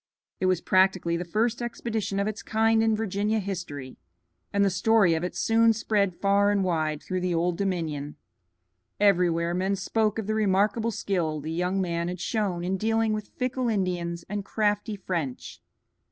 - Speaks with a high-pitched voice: Yes, high, 195 Hz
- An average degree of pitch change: Yes, average, 3.7 semitones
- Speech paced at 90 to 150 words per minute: No, average, 170 wpm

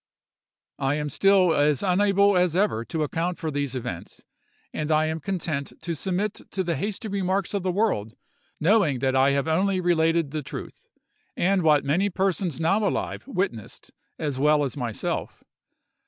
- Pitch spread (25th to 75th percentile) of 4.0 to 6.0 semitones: Yes, average, 4.9 semitones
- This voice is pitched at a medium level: Yes, medium, 165 Hz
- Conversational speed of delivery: Yes, average, 165 wpm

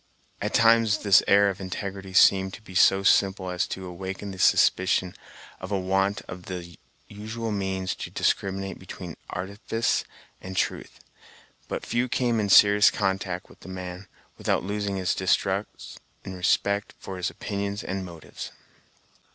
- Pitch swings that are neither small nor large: No, narrow, 1.6 semitones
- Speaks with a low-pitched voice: Yes, very low, 95 Hz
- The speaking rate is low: No, average, 150 wpm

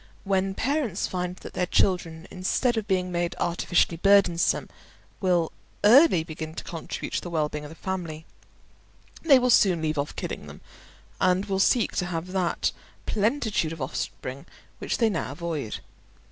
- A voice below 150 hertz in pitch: No, medium, 180 Hz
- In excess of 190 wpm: No, average, 160 wpm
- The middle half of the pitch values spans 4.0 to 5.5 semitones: No, average, 3.4 semitones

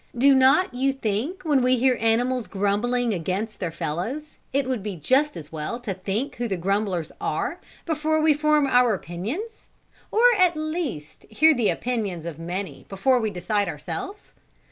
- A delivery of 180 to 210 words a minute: No, average, 165 wpm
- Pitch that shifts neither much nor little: No, wide, 6.4 semitones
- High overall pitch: Yes, high, 245 Hz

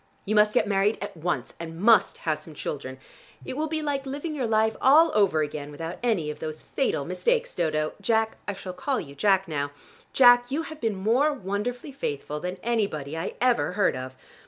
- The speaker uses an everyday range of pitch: No, wide, 7.6 semitones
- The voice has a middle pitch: No, high, 205 Hz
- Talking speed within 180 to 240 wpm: Yes, average, 200 wpm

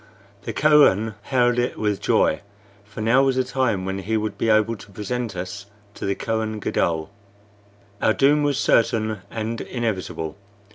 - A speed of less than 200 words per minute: Yes, average, 160 wpm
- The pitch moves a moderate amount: Yes, average, 3.4 semitones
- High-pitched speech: No, low, 110 Hz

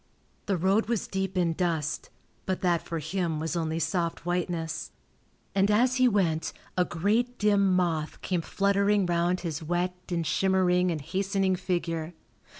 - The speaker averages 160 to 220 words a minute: No, average, 150 wpm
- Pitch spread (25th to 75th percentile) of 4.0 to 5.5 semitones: No, average, 2.7 semitones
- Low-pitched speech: No, medium, 180 Hz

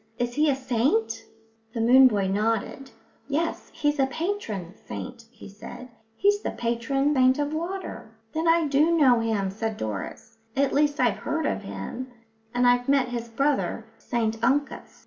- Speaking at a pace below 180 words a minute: Yes, average, 165 wpm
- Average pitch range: Yes, average, 4.4 semitones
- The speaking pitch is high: Yes, very high, 250 Hz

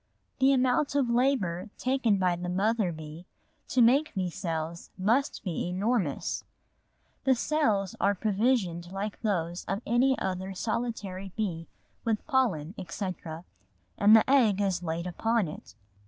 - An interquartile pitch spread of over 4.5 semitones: Yes, average, 5.0 semitones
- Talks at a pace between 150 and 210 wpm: No, average, 140 wpm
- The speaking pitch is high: Yes, high, 200 Hz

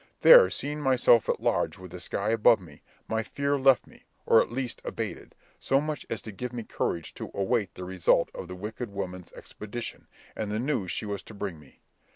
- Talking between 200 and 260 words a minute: Yes, fast, 205 wpm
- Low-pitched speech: Yes, low, 110 Hz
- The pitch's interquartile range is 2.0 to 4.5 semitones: No, average, 5.1 semitones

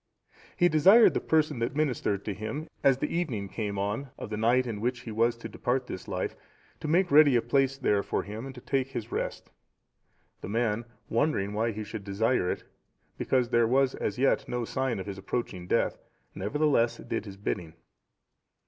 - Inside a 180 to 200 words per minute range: Yes, average, 190 wpm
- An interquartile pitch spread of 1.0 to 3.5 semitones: No, average, 4.6 semitones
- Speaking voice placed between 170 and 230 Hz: No, low, 120 Hz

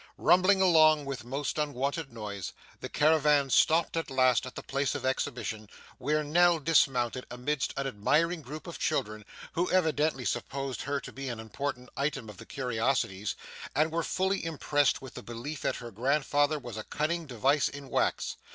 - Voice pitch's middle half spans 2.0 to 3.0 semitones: No, average, 3.9 semitones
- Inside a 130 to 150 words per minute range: No, average, 170 wpm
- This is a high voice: No, medium, 140 Hz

